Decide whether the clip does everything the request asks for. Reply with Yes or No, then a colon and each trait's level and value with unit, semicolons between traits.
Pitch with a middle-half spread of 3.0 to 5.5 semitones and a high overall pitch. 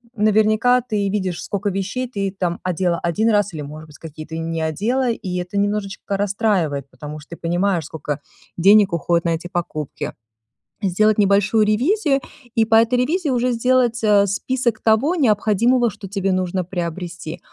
Yes: average, 4.5 semitones; high, 200 Hz